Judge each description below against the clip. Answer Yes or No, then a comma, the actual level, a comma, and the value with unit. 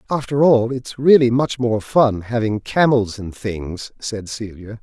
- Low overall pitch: Yes, low, 115 Hz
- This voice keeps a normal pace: Yes, average, 160 wpm